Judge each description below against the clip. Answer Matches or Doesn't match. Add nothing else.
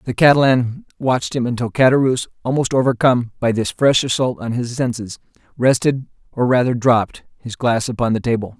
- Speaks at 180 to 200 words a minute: Doesn't match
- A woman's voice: Doesn't match